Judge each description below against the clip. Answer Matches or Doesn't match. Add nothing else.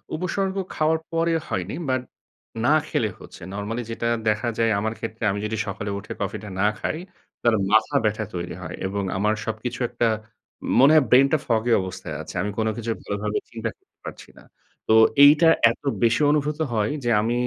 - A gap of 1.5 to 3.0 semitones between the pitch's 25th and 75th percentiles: Doesn't match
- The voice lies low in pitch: Matches